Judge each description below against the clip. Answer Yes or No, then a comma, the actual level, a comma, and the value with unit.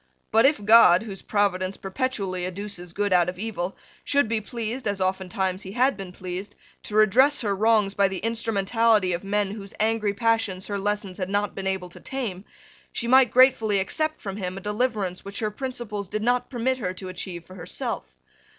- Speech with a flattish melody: No, average, 3.2 semitones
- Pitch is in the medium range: No, high, 205 Hz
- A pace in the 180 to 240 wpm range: Yes, average, 190 wpm